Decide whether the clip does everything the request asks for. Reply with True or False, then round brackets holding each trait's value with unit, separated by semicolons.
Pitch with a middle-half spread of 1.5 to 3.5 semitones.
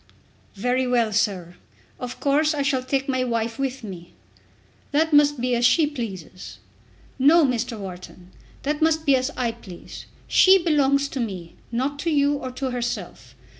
False (3.9 semitones)